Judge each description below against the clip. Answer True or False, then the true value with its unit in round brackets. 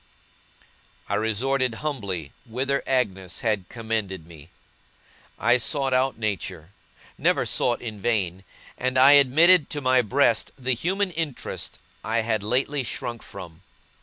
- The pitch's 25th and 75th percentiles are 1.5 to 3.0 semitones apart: False (4.6 semitones)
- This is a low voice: True (120 Hz)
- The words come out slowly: True (130 wpm)